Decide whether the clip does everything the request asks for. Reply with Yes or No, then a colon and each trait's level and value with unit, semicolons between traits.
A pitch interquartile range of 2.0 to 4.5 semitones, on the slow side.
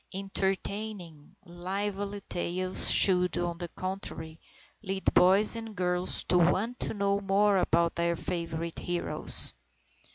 Yes: narrow, 2.4 semitones; slow, 120 wpm